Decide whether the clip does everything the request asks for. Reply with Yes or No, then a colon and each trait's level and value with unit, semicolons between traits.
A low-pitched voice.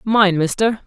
No: high, 200 Hz